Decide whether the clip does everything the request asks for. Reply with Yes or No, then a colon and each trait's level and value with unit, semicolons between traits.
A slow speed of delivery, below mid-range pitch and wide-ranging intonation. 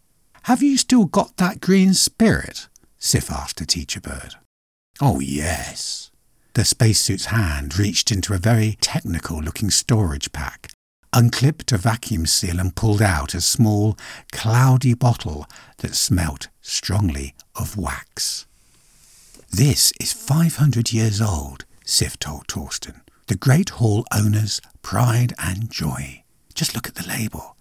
Yes: slow, 130 wpm; low, 110 Hz; wide, 5.8 semitones